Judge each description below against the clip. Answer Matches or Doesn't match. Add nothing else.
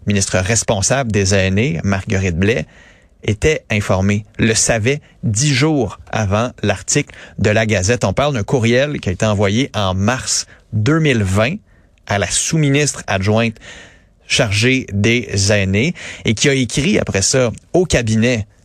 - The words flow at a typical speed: Doesn't match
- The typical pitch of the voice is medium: Doesn't match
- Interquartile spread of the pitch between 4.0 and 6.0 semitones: Matches